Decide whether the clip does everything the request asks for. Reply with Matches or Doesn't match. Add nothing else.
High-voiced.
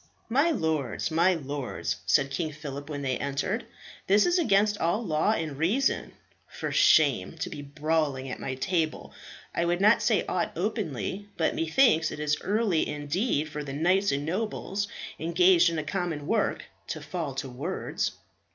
Doesn't match